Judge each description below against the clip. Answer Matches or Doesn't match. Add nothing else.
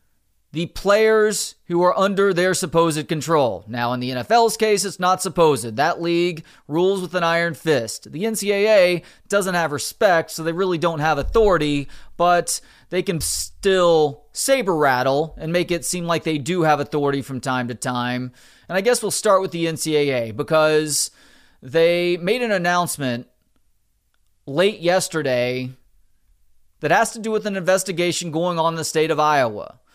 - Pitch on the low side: Doesn't match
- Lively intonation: Doesn't match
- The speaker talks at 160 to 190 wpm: Matches